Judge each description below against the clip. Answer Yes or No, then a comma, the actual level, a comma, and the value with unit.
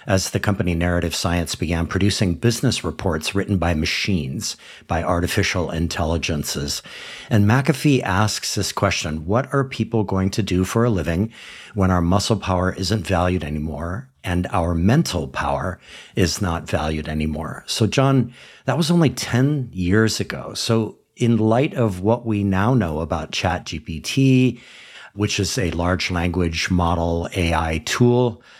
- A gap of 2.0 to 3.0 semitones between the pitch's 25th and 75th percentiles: No, average, 5.0 semitones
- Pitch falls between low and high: No, very low, 95 Hz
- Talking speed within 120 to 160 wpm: Yes, average, 145 wpm